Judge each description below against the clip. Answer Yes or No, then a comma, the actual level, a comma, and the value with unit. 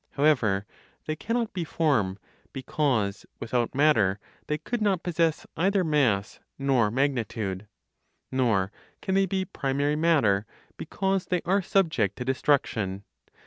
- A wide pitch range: Yes, wide, 7.5 semitones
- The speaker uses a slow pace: Yes, slow, 125 wpm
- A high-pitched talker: No, medium, 140 Hz